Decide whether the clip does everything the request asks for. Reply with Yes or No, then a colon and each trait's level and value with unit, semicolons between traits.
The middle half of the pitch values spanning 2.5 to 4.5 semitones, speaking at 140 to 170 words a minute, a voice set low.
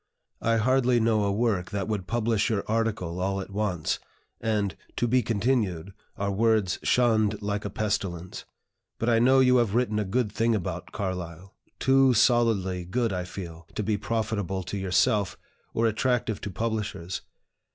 Yes: average, 3.2 semitones; average, 160 wpm; low, 105 Hz